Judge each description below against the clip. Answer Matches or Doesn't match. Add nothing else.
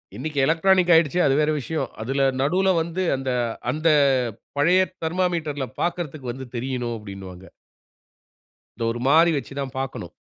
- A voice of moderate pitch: Matches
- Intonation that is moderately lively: Matches